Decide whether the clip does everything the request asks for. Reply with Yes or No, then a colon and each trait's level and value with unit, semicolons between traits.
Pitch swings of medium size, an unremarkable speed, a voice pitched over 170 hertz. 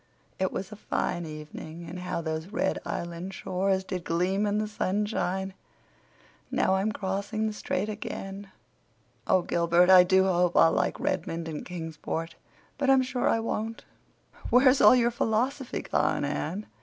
Yes: average, 3.7 semitones; average, 155 wpm; high, 190 Hz